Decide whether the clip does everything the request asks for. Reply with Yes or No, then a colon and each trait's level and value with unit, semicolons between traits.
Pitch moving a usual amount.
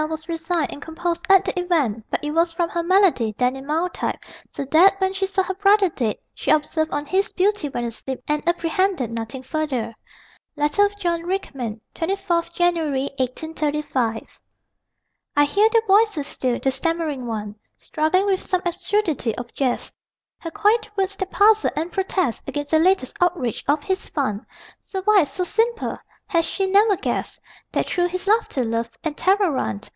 No: wide, 5.7 semitones